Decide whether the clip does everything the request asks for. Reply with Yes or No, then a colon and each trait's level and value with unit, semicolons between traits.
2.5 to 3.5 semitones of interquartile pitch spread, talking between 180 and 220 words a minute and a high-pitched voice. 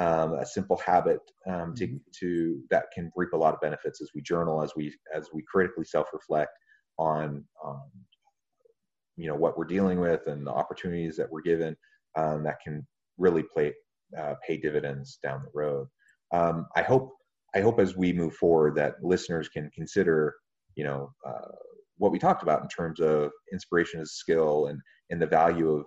No: average, 3.0 semitones; average, 185 wpm; very low, 85 Hz